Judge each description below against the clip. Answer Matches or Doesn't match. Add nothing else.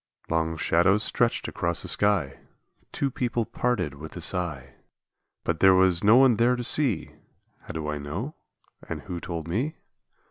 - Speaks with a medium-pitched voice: Doesn't match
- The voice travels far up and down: Matches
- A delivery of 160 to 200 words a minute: Matches